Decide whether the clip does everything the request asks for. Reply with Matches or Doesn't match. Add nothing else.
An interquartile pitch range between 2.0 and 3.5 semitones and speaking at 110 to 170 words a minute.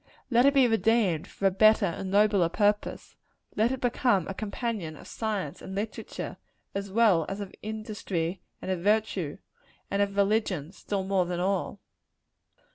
Matches